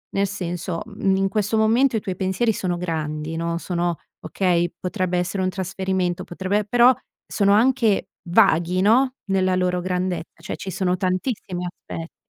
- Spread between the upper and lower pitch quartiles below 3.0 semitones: Yes, narrow, 2.6 semitones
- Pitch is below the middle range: No, medium, 185 Hz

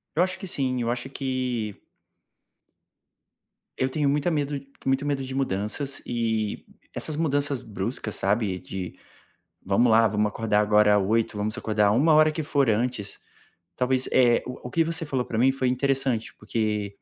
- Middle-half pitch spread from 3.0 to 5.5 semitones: Yes, average, 4.5 semitones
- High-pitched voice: No, low, 125 Hz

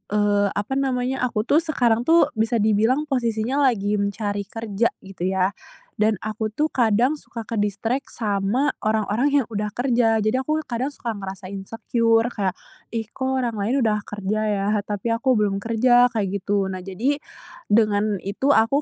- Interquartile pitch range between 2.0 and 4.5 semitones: Yes, average, 3.3 semitones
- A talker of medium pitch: No, high, 220 Hz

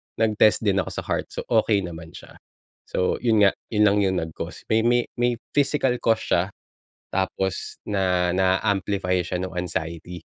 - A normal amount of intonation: Yes, average, 3.5 semitones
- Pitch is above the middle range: No, very low, 95 Hz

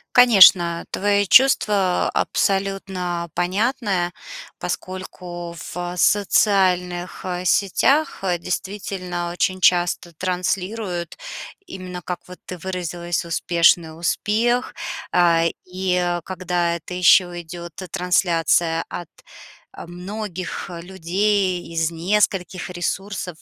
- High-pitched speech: No, medium, 180 Hz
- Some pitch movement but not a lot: No, narrow, 1.9 semitones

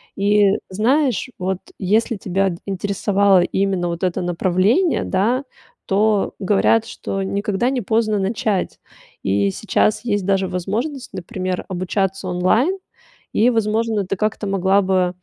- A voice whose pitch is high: Yes, high, 195 Hz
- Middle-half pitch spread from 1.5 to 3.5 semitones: Yes, average, 2.7 semitones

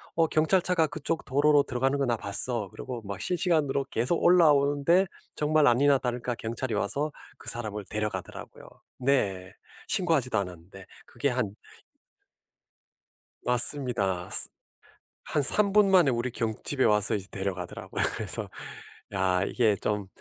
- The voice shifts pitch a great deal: Yes, wide, 6.0 semitones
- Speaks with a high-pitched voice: No, low, 125 Hz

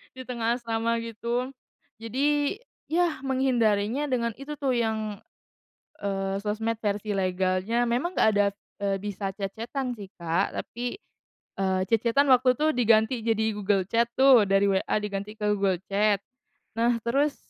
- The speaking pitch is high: Yes, high, 225 Hz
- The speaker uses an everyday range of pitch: Yes, average, 3.9 semitones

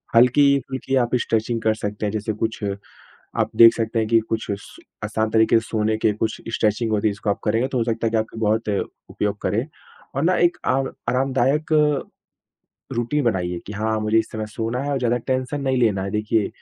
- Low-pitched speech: Yes, low, 115 Hz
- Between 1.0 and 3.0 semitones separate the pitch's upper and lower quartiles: Yes, average, 2.7 semitones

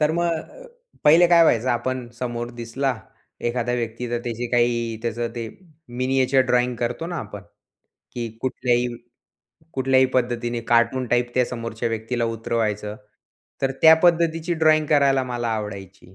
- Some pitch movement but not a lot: No, narrow, 2.3 semitones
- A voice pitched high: No, low, 120 Hz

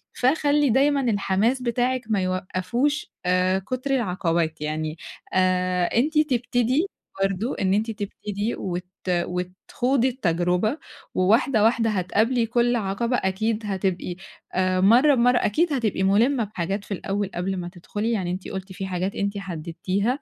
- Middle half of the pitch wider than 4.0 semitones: Yes, average, 4.8 semitones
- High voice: Yes, high, 200 Hz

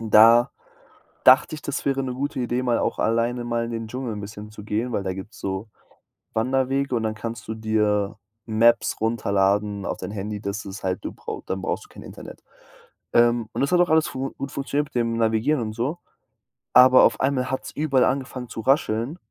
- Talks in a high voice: No, low, 115 Hz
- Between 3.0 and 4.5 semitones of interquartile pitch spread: Yes, average, 3.4 semitones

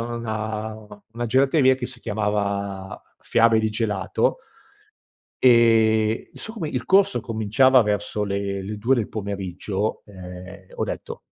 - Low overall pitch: Yes, low, 110 Hz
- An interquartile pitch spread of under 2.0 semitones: No, average, 2.8 semitones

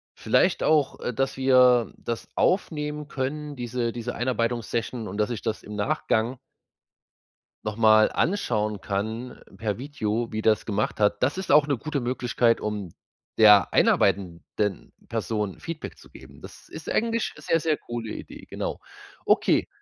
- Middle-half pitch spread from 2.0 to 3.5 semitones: No, average, 4.1 semitones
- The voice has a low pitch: Yes, low, 120 Hz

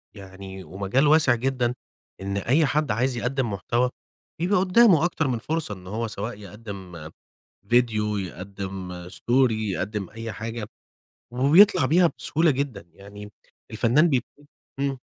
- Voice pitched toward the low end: Yes, low, 115 Hz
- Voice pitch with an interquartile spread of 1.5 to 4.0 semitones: No, wide, 5.6 semitones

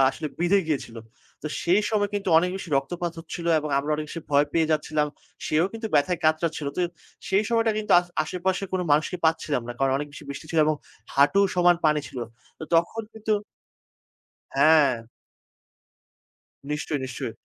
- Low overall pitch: No, medium, 160 Hz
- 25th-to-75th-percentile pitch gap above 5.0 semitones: No, average, 3.3 semitones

